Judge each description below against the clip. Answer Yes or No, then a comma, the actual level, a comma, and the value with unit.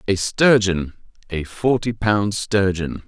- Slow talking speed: Yes, slow, 115 wpm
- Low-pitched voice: Yes, low, 100 Hz